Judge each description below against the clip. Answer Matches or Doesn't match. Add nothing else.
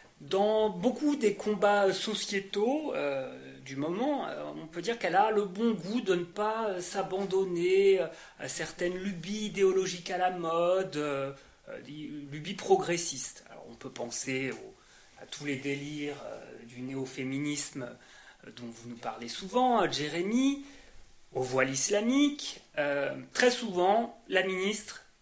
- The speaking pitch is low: Doesn't match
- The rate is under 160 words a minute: Matches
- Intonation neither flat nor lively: Doesn't match